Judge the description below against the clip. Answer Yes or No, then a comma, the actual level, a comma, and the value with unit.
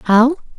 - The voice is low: No, high, 245 Hz